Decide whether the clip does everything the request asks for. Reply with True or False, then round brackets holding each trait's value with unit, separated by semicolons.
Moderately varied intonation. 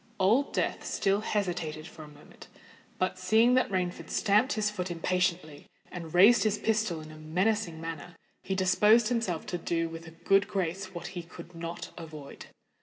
True (3.8 semitones)